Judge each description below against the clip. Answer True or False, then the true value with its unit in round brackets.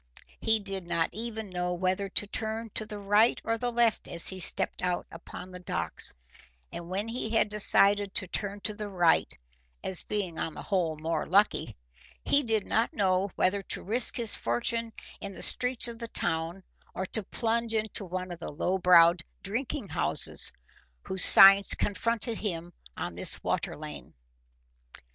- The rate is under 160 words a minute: False (170 wpm)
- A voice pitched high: True (200 Hz)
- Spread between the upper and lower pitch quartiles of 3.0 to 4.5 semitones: True (3.7 semitones)